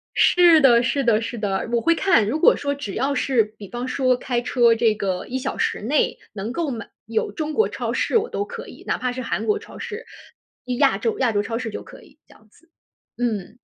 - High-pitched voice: Yes, very high, 250 Hz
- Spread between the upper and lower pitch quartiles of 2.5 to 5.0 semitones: No, wide, 5.4 semitones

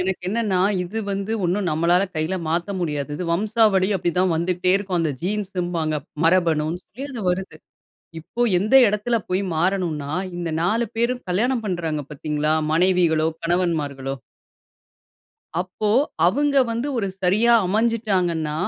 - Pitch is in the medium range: Yes, medium, 180 Hz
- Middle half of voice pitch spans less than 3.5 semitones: No, average, 4.0 semitones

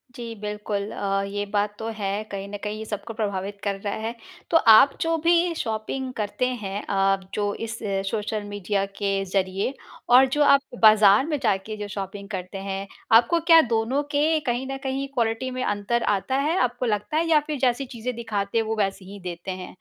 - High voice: Yes, high, 215 Hz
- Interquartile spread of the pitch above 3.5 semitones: Yes, average, 3.9 semitones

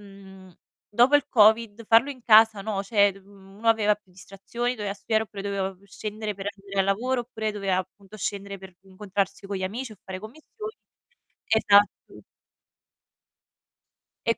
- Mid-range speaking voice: No, high, 205 Hz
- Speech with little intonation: Yes, narrow, 2.1 semitones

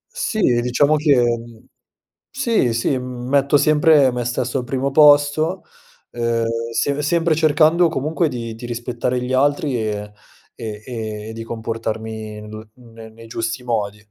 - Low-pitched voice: Yes, low, 125 Hz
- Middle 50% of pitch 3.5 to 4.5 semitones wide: Yes, average, 4.2 semitones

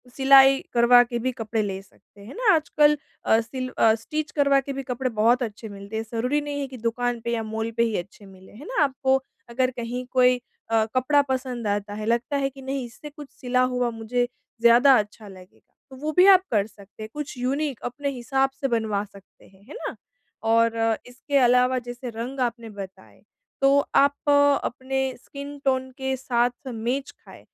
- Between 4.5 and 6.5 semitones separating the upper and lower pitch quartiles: No, average, 3.3 semitones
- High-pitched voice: Yes, high, 245 Hz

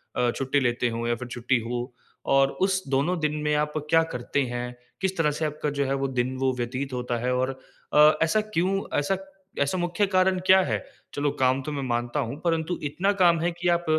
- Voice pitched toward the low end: No, medium, 145 Hz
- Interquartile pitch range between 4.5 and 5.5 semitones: Yes, average, 5.1 semitones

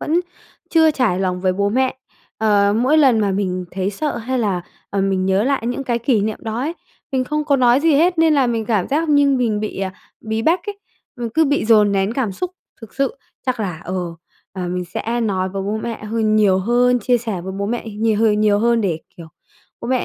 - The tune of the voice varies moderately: Yes, average, 4.7 semitones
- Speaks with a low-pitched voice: No, high, 225 Hz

